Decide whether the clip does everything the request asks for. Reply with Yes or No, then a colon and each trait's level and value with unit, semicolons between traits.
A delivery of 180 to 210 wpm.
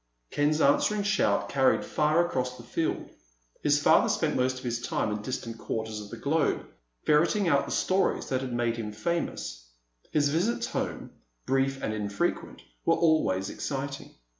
No: average, 165 wpm